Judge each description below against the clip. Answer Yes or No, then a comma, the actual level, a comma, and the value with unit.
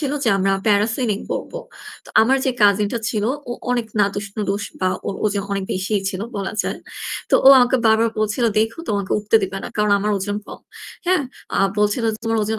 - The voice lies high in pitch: Yes, high, 210 Hz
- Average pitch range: No, narrow, 2.2 semitones